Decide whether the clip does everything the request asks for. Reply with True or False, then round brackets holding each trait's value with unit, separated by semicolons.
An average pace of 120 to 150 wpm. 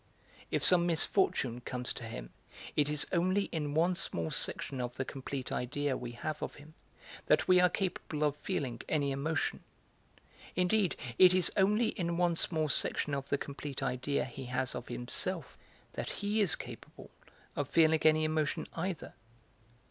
False (165 wpm)